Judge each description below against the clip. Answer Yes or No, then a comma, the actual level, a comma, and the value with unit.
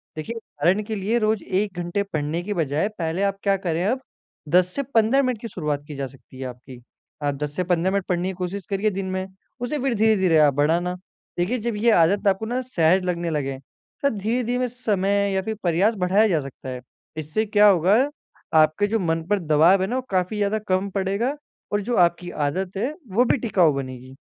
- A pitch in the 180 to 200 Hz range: Yes, high, 190 Hz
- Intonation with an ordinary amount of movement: Yes, average, 4.7 semitones